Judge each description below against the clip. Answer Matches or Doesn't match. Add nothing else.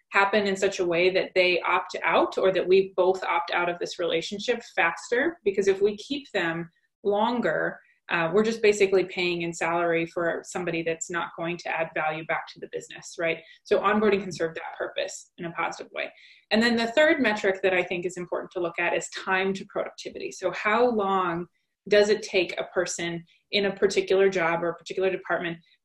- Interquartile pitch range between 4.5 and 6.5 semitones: Doesn't match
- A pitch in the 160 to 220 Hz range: Matches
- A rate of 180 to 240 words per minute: Matches